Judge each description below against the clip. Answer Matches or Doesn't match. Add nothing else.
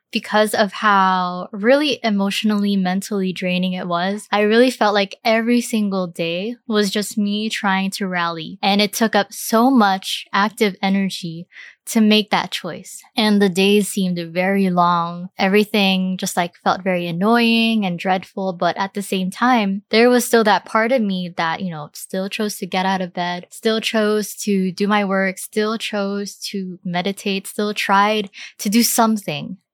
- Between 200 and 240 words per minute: Doesn't match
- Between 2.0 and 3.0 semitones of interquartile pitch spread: Matches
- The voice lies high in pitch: Matches